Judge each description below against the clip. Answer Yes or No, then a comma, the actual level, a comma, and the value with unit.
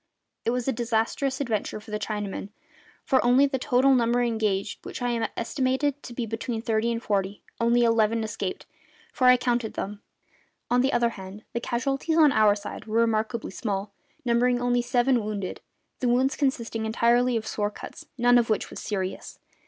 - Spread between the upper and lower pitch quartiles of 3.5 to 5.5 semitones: No, narrow, 2.4 semitones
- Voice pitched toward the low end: No, high, 235 Hz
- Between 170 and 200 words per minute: Yes, average, 175 wpm